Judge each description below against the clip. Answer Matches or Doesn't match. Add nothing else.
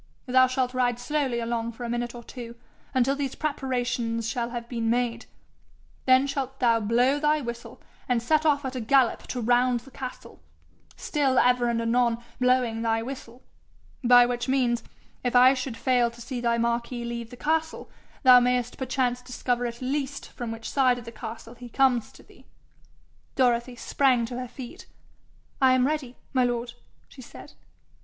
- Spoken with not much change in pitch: Matches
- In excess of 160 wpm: Matches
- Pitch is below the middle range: Doesn't match